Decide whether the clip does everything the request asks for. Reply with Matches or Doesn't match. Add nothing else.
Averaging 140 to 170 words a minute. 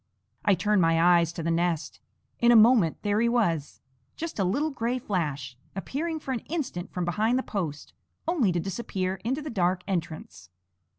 Doesn't match